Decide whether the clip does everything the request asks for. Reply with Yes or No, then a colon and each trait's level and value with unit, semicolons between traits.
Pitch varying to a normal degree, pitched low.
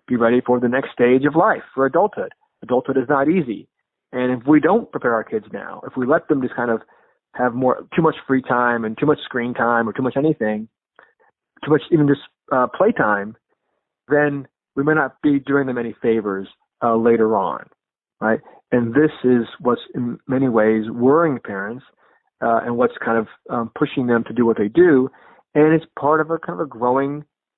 Yes: average, 3.9 semitones; low, 130 Hz